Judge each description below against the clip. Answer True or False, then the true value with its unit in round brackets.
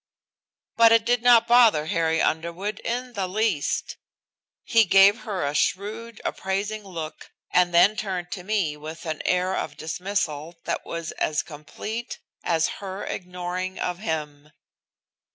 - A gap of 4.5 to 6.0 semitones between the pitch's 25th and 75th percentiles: True (4.8 semitones)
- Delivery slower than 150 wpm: True (140 wpm)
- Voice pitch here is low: False (185 Hz)